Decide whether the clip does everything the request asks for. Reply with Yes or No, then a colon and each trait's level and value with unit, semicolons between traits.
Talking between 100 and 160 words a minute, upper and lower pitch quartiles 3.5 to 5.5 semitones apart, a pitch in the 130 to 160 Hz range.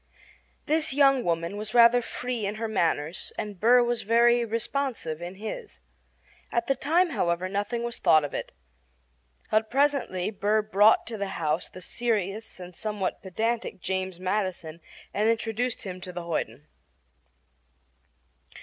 No: average, 145 wpm; average, 4.5 semitones; high, 215 Hz